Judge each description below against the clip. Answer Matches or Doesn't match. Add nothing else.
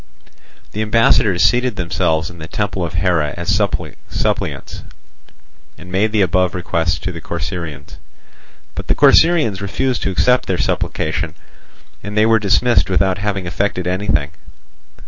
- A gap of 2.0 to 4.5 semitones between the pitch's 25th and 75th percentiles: Matches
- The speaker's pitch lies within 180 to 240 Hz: Doesn't match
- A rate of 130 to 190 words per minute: Matches